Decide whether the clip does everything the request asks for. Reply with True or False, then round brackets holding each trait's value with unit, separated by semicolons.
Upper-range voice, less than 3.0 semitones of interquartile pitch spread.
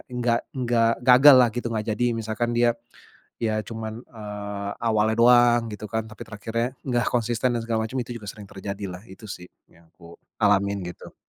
False (110 Hz; 2.5 semitones)